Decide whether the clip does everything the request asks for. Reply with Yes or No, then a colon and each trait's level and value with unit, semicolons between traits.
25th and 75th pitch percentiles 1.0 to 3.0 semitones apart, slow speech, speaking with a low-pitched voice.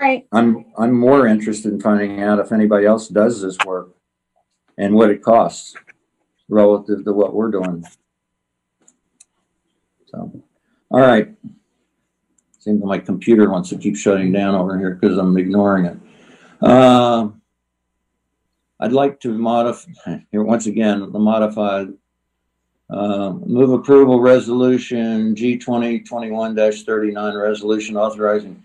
Yes: average, 2.7 semitones; slow, 120 wpm; low, 105 Hz